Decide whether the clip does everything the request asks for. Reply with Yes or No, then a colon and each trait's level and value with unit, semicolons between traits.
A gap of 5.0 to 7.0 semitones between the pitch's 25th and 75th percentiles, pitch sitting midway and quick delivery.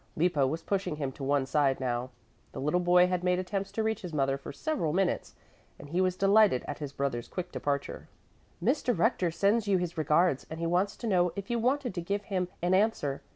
Yes: wide, 5.4 semitones; medium, 180 Hz; fast, 220 wpm